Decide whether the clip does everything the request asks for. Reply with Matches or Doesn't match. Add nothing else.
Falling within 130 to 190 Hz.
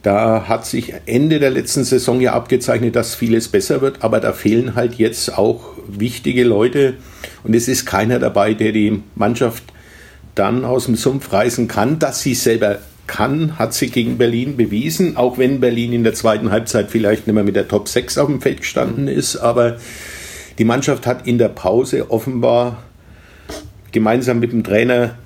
Doesn't match